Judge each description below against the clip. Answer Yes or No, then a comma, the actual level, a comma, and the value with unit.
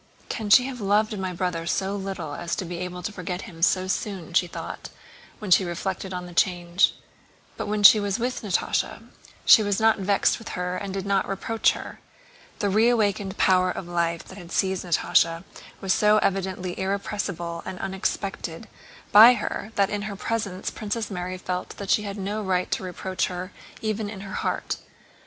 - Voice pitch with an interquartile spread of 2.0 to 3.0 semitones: Yes, narrow, 2.4 semitones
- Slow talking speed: No, average, 185 wpm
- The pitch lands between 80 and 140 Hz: No, high, 190 Hz